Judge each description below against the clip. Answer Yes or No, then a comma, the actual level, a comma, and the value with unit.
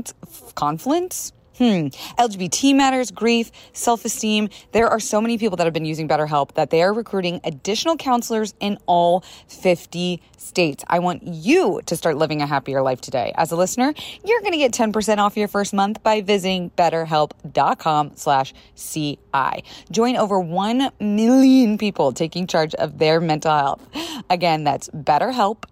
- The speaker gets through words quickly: No, average, 155 wpm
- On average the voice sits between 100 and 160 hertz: No, medium, 185 Hz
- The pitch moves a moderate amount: No, wide, 6.2 semitones